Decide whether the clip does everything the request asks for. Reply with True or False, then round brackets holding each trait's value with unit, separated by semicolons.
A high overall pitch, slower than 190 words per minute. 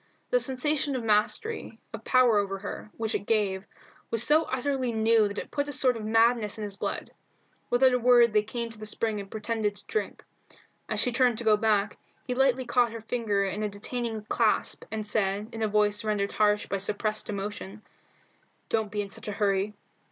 False (220 Hz; 205 wpm)